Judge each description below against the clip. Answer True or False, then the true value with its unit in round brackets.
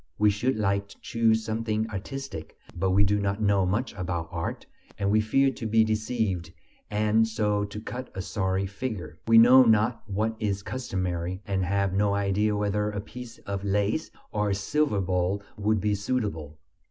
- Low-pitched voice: True (105 Hz)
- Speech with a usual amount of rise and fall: False (2.3 semitones)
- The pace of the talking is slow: False (175 wpm)